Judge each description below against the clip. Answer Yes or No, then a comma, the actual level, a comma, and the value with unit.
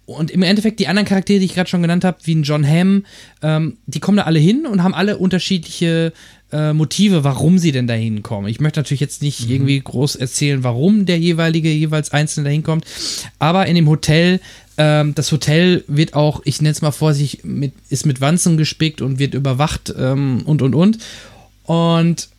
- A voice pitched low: No, medium, 155 Hz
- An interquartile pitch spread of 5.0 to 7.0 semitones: No, average, 3.6 semitones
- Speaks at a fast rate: Yes, fast, 205 wpm